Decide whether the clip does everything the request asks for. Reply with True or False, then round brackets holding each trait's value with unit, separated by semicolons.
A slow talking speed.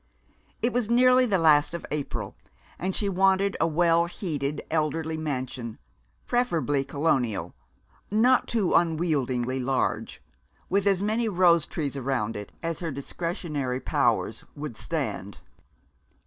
True (125 wpm)